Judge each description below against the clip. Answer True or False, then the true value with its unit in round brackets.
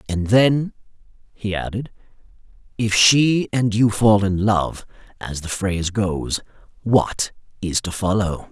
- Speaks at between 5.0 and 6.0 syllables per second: False (3.8 syllables/s)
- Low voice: True (105 Hz)